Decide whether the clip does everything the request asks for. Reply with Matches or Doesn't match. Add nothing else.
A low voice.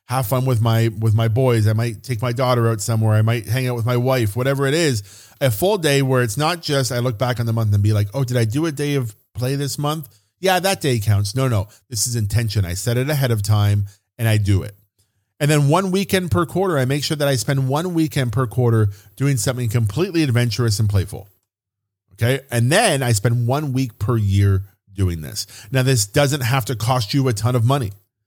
Matches